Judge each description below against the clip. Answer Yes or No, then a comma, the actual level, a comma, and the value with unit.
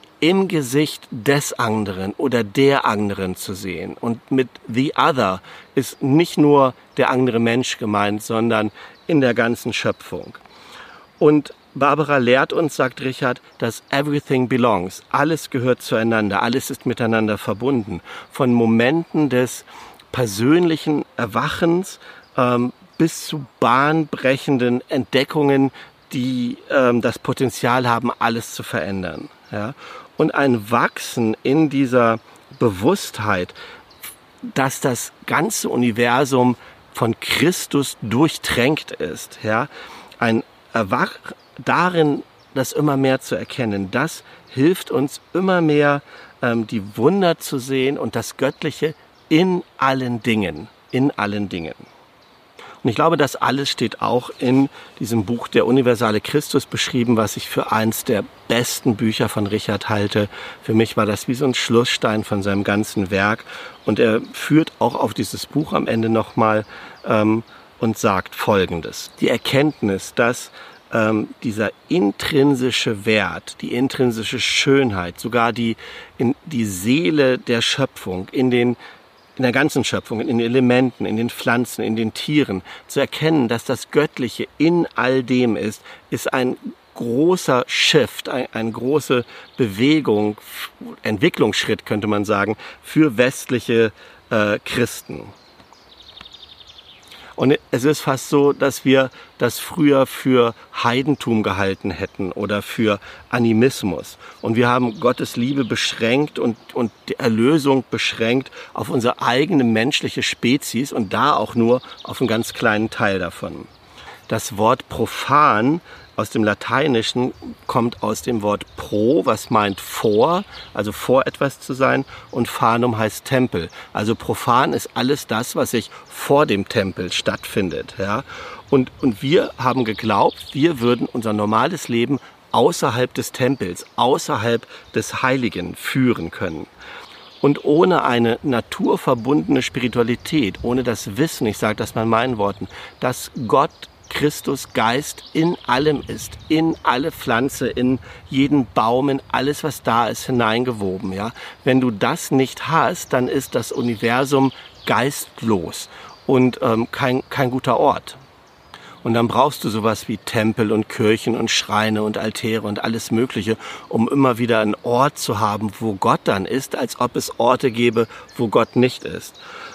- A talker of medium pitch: No, low, 120 Hz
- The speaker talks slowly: No, average, 140 wpm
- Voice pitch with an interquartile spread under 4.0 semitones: Yes, average, 3.6 semitones